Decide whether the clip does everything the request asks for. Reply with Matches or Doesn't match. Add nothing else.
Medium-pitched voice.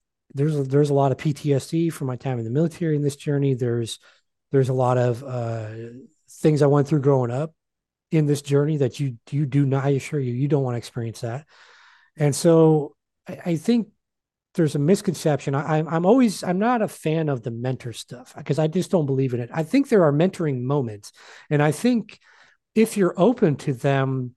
Matches